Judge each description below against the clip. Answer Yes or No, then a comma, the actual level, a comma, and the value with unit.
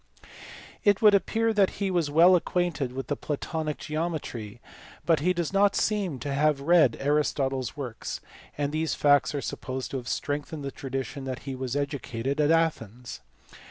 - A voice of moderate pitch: Yes, medium, 145 Hz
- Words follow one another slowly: No, average, 165 wpm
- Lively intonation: No, average, 4.0 semitones